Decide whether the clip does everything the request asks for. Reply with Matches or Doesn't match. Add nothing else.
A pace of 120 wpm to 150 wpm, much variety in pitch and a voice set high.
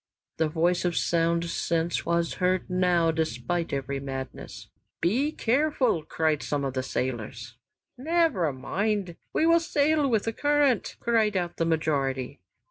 Doesn't match